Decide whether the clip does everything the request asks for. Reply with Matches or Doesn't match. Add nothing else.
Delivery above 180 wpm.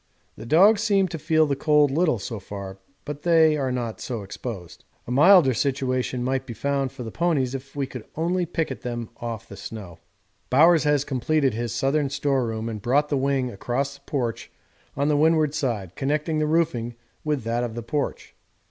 Matches